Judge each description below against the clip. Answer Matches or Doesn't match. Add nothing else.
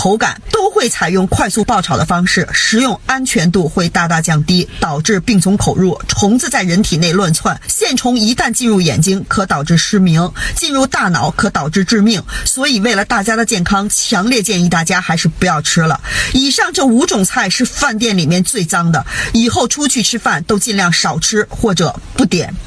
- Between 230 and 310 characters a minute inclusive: Matches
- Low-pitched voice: Doesn't match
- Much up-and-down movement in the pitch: Doesn't match